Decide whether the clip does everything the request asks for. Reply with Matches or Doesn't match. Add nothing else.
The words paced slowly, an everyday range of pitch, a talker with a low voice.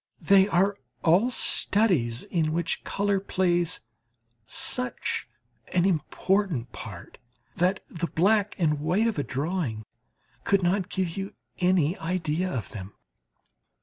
Doesn't match